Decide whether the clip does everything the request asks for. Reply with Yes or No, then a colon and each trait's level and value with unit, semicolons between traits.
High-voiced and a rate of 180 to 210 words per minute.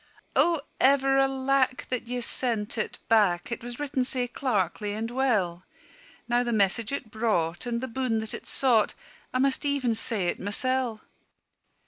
No: high, 240 Hz; average, 160 wpm